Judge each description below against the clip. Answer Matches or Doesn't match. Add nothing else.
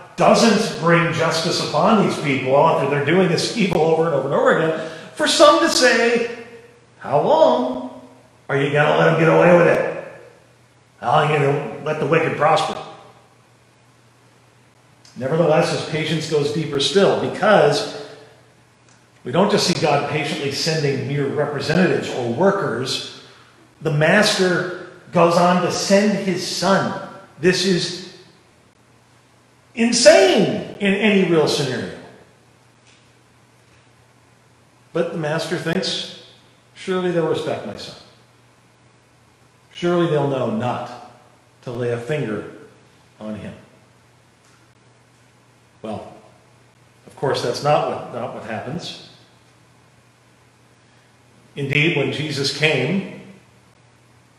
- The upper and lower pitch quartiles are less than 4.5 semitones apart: Doesn't match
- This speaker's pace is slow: Matches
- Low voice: Doesn't match